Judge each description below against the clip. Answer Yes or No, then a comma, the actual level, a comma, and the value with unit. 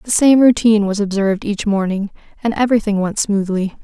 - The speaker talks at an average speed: Yes, average, 170 wpm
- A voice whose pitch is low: No, high, 210 Hz